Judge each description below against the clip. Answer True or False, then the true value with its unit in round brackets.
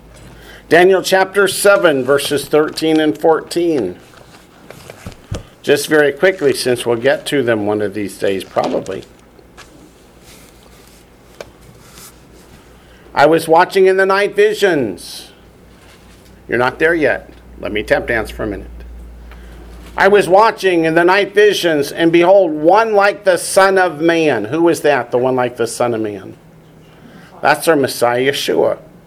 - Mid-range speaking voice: True (160 Hz)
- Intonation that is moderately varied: False (7.8 semitones)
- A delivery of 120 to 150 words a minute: True (140 wpm)